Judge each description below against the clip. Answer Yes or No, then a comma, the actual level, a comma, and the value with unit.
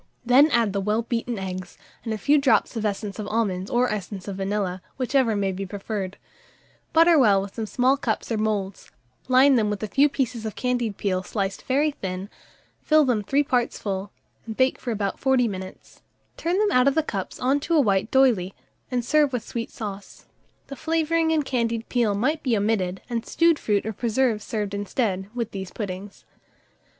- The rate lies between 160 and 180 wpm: No, average, 190 wpm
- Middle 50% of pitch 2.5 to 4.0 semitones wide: No, average, 4.7 semitones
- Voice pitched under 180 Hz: No, high, 225 Hz